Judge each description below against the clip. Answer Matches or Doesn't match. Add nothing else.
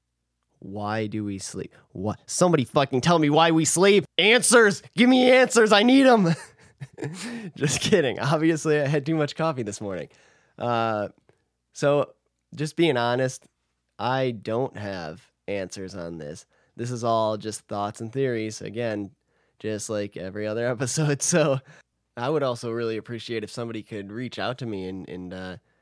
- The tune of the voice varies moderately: Doesn't match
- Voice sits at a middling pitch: Doesn't match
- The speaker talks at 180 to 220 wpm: Doesn't match